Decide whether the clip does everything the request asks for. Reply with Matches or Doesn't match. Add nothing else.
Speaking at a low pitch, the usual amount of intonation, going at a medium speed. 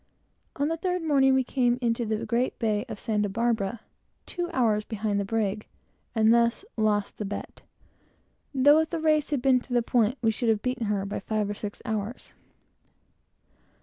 Doesn't match